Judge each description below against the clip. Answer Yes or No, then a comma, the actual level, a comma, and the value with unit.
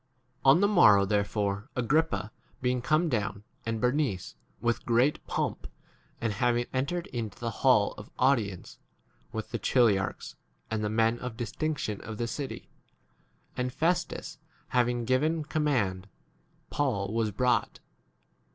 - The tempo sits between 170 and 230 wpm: No, slow, 135 wpm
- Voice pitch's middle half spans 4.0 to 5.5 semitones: Yes, average, 4.5 semitones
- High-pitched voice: No, low, 120 Hz